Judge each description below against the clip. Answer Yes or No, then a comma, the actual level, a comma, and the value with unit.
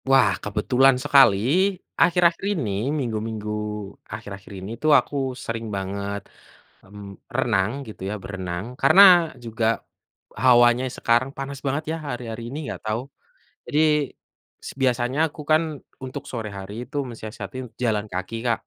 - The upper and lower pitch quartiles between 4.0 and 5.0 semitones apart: Yes, average, 4.6 semitones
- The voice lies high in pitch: No, low, 115 Hz